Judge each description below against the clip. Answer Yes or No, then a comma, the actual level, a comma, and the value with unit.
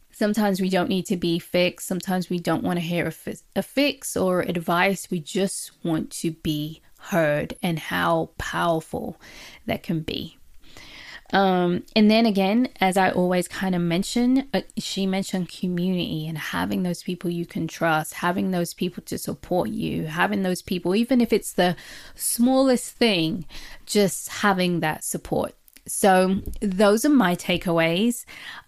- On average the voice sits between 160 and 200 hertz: Yes, medium, 185 Hz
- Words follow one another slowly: No, average, 160 wpm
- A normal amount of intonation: Yes, average, 3.0 semitones